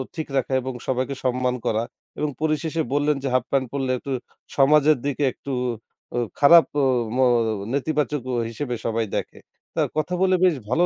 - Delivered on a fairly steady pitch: No, average, 3.1 semitones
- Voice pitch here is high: No, medium, 140 Hz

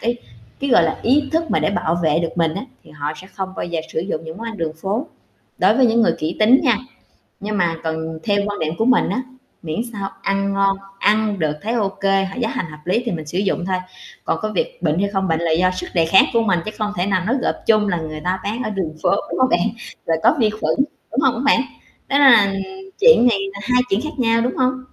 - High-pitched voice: Yes, high, 200 Hz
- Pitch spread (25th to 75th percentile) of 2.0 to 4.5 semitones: No, average, 5.1 semitones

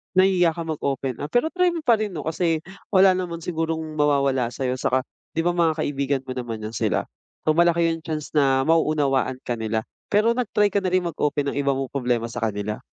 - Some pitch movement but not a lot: Yes, average, 4.6 semitones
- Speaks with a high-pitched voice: No, medium, 155 Hz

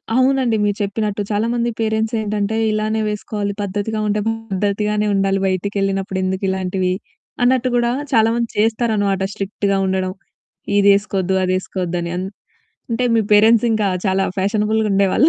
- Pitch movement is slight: Yes, narrow, 2.2 semitones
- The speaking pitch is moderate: No, high, 205 Hz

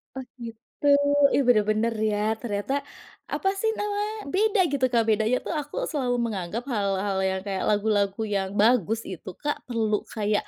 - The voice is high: Yes, high, 220 Hz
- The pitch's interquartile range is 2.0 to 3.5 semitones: No, average, 4.2 semitones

